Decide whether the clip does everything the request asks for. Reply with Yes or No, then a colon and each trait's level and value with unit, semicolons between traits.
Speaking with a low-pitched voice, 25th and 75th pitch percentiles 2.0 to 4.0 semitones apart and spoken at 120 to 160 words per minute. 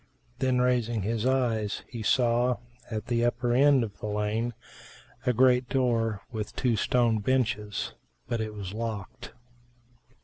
Yes: low, 115 Hz; narrow, 2.6 semitones; average, 140 wpm